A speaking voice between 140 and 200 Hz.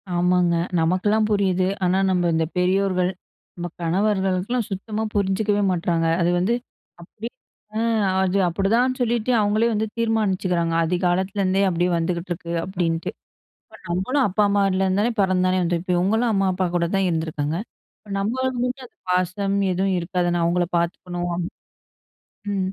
Yes: medium, 185 Hz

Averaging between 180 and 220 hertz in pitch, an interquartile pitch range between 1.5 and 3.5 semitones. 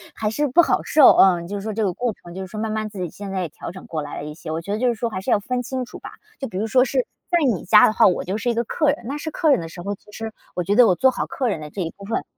No: high, 210 Hz; average, 5.0 semitones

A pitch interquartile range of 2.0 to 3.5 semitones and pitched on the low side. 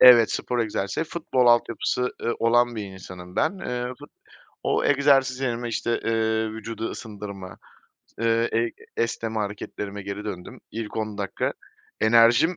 Yes: narrow, 2.6 semitones; low, 115 Hz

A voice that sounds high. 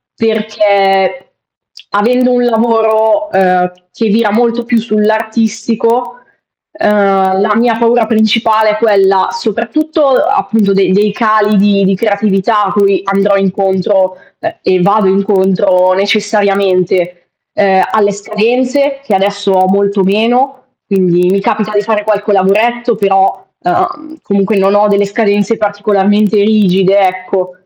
Yes: high, 205 Hz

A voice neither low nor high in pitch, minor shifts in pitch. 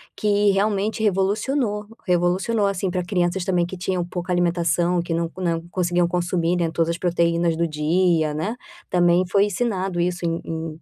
Yes: medium, 175 Hz; narrow, 2.2 semitones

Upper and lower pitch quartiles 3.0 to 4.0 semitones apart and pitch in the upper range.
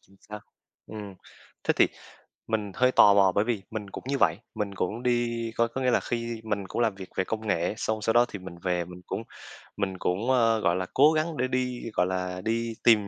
No: average, 3.7 semitones; low, 110 Hz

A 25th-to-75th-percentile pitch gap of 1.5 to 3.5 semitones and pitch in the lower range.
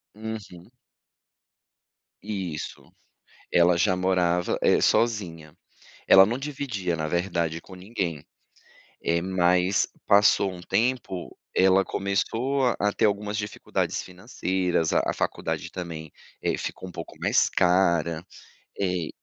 Yes: average, 3.0 semitones; very low, 95 Hz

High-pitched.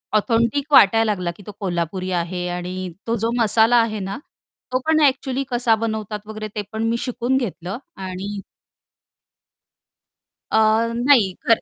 Yes: high, 215 Hz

